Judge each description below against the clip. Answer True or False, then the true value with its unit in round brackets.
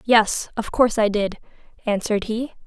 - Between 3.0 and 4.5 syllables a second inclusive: False (5.3 syllables/s)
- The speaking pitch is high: True (220 Hz)